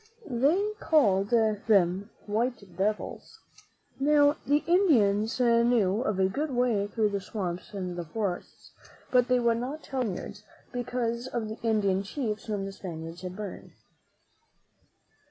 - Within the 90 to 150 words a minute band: Yes, average, 140 wpm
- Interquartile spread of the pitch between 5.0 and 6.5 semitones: No, average, 4.1 semitones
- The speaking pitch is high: Yes, high, 220 Hz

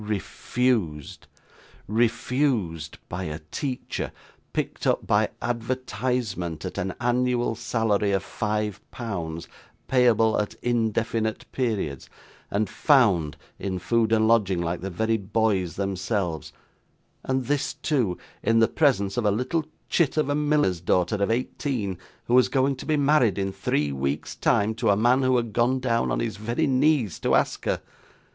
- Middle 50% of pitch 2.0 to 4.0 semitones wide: No, average, 4.6 semitones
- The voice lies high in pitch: No, low, 110 Hz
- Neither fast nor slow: Yes, average, 150 wpm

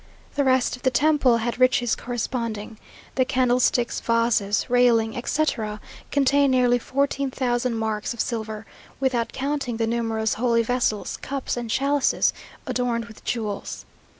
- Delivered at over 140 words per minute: No, slow, 135 wpm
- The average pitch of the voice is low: No, high, 240 Hz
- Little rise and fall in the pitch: Yes, narrow, 2.3 semitones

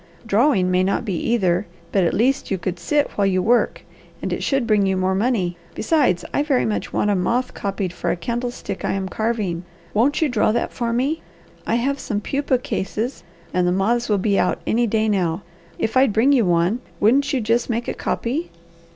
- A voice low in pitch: No, high, 220 Hz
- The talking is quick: Yes, fast, 210 wpm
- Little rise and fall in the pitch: No, average, 4.5 semitones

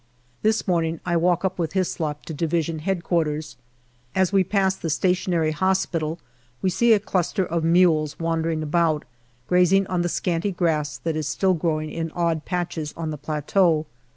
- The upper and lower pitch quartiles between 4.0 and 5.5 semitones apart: No, average, 2.7 semitones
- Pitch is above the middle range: No, medium, 170 Hz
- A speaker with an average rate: Yes, average, 160 wpm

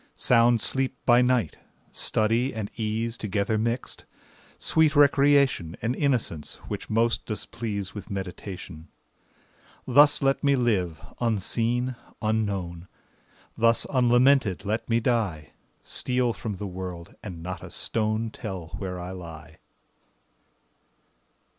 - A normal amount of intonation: Yes, average, 4.6 semitones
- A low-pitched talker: Yes, low, 110 Hz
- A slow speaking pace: Yes, slow, 115 wpm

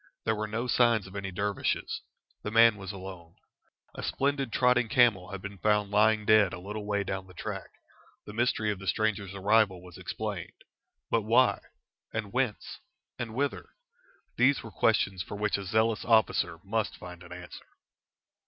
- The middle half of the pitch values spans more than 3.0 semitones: No, average, 2.7 semitones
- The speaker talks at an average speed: Yes, average, 170 wpm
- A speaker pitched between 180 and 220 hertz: No, low, 105 Hz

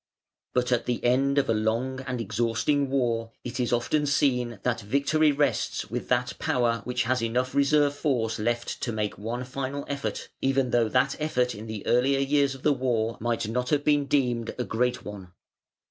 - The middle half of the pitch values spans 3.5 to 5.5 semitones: No, average, 3.0 semitones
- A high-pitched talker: No, low, 125 Hz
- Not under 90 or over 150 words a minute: No, average, 190 wpm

